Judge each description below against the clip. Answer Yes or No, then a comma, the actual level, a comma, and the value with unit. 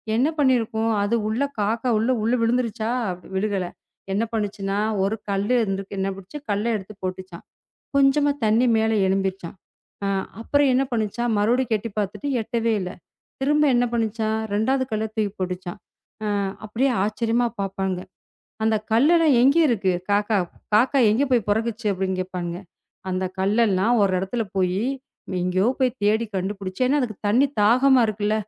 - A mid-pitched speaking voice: No, high, 215 Hz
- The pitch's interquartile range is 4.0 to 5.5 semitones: No, average, 3.5 semitones